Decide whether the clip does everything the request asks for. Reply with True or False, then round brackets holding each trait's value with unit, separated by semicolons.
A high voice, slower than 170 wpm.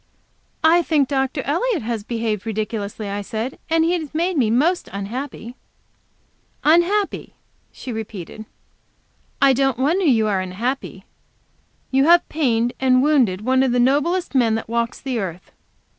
True (255 Hz; 145 wpm)